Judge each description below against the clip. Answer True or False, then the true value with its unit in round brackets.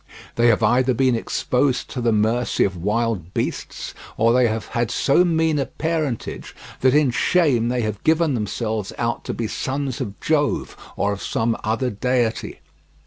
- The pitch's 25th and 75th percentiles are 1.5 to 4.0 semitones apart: True (3.3 semitones)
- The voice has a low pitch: True (120 Hz)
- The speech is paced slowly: False (170 wpm)